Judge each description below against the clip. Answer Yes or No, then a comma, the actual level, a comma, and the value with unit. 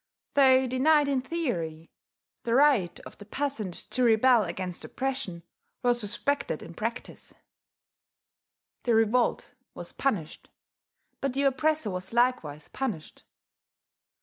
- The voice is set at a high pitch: Yes, high, 240 Hz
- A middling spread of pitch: No, wide, 6.1 semitones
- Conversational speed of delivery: No, slow, 115 wpm